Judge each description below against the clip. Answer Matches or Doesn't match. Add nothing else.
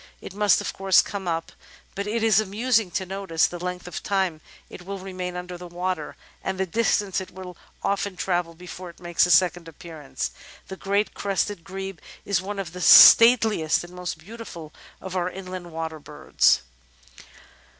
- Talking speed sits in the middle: Matches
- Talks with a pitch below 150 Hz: Doesn't match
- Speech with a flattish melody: Matches